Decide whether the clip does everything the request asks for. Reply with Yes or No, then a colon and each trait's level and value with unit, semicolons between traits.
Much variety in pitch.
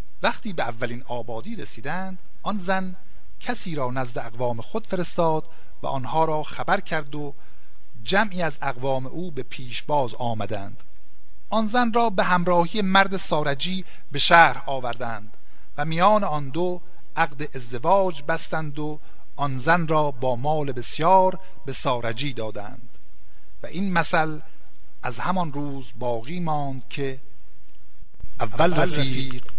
Yes: wide, 6.0 semitones